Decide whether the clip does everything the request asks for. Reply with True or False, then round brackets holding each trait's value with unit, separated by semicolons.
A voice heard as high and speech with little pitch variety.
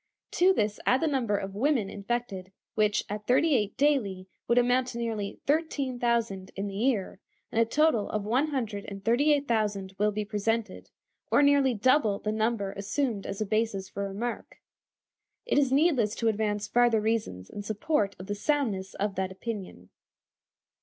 False (220 Hz; 4.1 semitones)